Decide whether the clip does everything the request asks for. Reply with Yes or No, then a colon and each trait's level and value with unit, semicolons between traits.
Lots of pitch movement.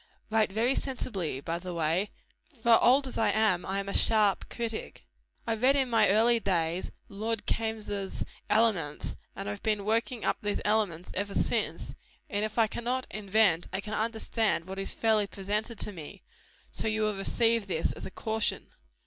No: average, 2.7 semitones